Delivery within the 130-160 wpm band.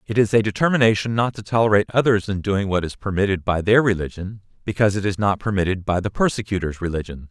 No: fast, 205 wpm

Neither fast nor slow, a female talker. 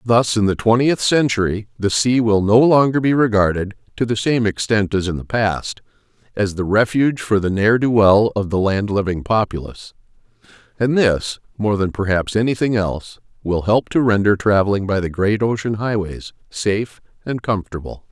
No: average, 175 wpm; male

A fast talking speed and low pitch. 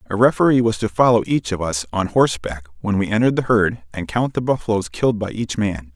Yes: fast, 230 wpm; low, 105 Hz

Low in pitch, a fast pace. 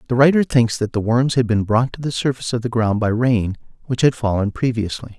Yes: low, 120 Hz; fast, 245 wpm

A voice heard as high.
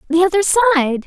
Yes: very high, 345 Hz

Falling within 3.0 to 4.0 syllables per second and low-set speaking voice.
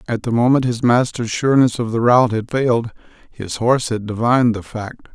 No: 5.8 syllables/s; low, 120 Hz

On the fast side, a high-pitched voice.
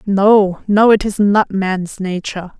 No: average, 160 wpm; high, 200 Hz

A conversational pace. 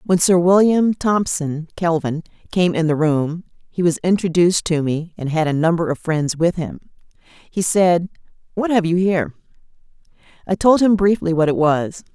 Yes: average, 175 wpm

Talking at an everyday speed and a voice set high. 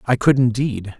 No: average, 180 wpm; low, 120 Hz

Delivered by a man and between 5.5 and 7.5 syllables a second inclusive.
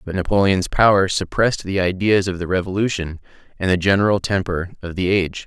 Yes: male; 6.0 syllables/s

